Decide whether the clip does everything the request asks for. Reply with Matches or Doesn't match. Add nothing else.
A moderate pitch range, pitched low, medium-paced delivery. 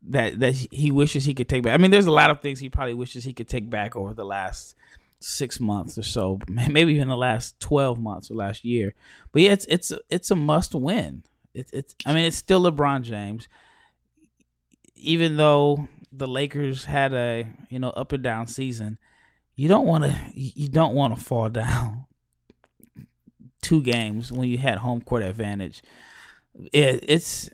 Matches